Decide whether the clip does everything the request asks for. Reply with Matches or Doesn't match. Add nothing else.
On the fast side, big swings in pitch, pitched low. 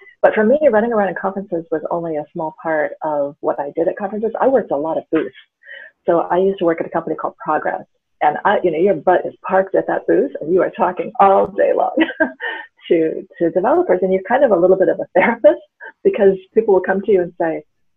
Doesn't match